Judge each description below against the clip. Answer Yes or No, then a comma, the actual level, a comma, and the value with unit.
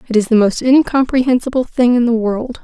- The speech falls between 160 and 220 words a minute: Yes, fast, 205 wpm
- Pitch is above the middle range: Yes, high, 240 Hz